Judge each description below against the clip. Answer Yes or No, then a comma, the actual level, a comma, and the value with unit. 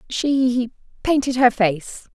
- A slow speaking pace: Yes, slow, 110 wpm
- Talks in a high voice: Yes, high, 245 Hz